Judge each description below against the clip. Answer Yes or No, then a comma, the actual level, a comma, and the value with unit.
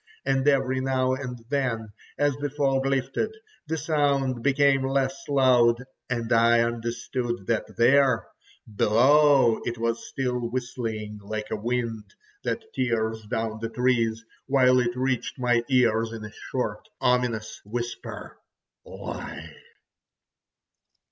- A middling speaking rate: No, slow, 115 wpm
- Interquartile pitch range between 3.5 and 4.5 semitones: No, average, 2.7 semitones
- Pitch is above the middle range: No, low, 125 Hz